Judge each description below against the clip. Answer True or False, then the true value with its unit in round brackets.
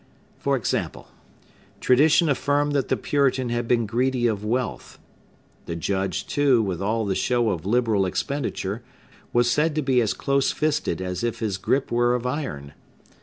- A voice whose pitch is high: False (120 Hz)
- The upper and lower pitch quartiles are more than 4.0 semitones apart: True (5.1 semitones)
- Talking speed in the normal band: True (165 wpm)